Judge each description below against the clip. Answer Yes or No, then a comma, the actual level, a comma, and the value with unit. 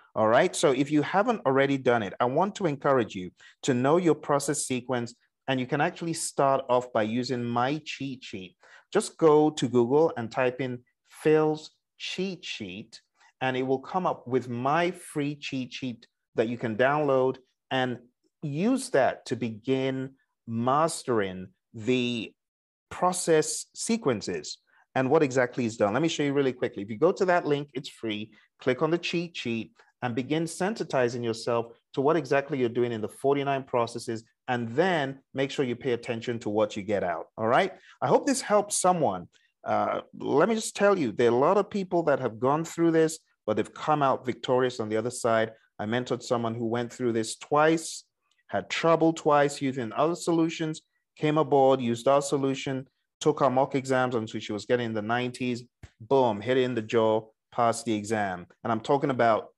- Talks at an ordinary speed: Yes, average, 190 wpm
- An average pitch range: Yes, average, 4.5 semitones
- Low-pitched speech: Yes, low, 130 Hz